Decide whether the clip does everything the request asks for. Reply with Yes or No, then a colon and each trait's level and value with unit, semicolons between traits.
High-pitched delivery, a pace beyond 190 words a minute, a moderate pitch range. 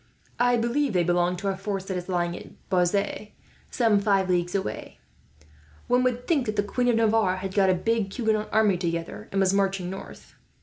Yes: high, 195 Hz; average, 200 wpm; average, 3.5 semitones